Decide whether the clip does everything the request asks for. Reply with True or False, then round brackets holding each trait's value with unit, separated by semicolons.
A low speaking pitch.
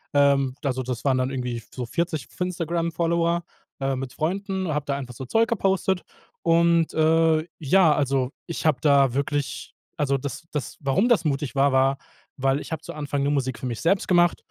False (145 Hz)